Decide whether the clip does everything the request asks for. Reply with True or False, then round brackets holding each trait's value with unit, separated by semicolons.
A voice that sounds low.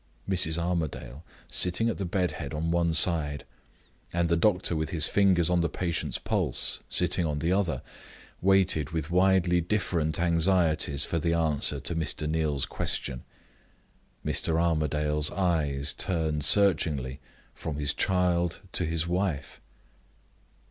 True (85 Hz)